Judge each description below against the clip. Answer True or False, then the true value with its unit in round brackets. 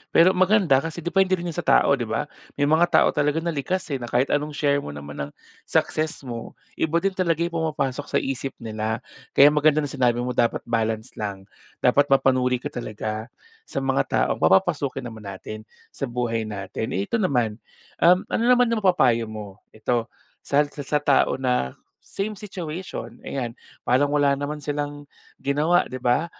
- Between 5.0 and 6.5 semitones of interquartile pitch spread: True (5.3 semitones)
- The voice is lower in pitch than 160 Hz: True (140 Hz)